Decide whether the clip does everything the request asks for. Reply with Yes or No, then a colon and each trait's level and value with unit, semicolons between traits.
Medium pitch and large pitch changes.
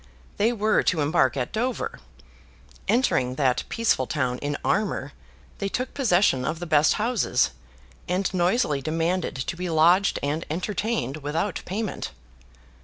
Yes: medium, 175 Hz; wide, 6.5 semitones